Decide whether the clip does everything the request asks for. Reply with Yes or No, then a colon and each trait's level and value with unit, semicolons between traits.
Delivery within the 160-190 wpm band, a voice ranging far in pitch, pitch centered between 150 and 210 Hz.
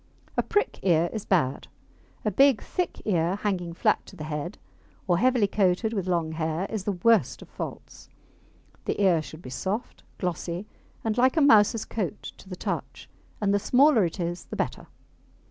No: average, 180 wpm; average, 4.3 semitones; high, 190 Hz